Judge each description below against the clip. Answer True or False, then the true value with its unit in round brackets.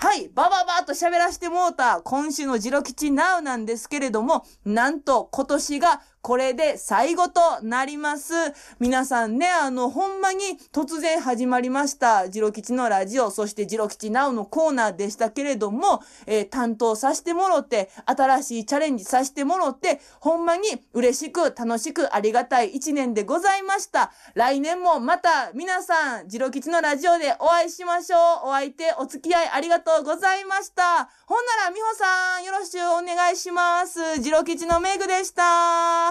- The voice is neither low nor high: False (300 Hz)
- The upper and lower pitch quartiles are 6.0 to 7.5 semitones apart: False (5.6 semitones)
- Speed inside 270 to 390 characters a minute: True (350 characters per minute)